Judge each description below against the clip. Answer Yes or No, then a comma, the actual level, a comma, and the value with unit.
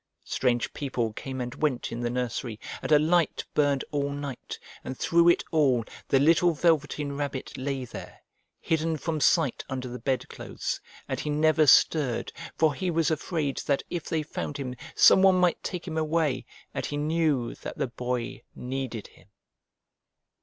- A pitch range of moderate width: Yes, average, 3.8 semitones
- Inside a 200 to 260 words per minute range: No, average, 165 wpm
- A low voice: No, medium, 145 Hz